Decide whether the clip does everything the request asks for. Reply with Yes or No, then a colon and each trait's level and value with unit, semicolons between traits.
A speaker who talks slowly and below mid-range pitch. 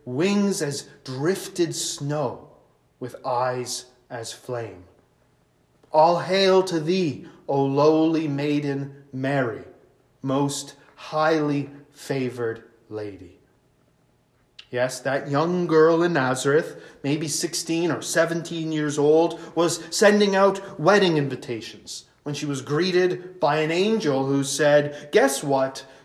No: slow, 110 wpm; medium, 145 Hz